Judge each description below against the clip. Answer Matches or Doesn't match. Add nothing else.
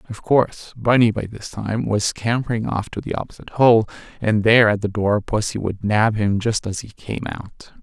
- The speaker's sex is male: Matches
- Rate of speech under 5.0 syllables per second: Doesn't match